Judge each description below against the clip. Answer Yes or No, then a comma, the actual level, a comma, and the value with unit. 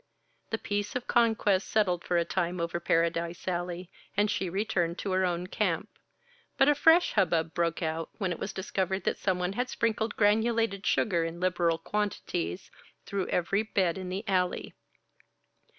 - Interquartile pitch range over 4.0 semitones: No, average, 3.3 semitones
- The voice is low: No, medium, 185 Hz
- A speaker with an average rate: Yes, average, 165 wpm